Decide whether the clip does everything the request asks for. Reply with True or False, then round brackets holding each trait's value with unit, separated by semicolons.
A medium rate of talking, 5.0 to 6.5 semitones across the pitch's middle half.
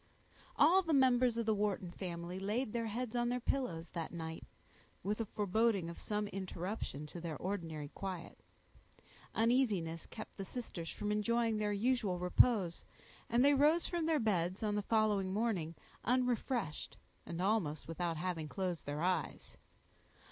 True (155 wpm; 5.3 semitones)